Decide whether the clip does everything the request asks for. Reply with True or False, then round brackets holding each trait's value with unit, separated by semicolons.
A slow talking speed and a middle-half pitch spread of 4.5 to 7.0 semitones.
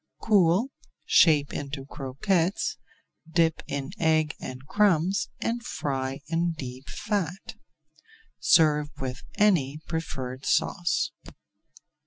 True (95 wpm; 4.8 semitones)